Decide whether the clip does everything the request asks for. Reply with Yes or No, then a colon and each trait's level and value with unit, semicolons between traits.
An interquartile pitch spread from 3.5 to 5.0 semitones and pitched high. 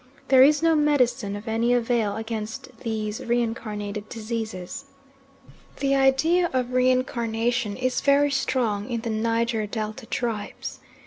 No: average, 2.9 semitones; high, 235 Hz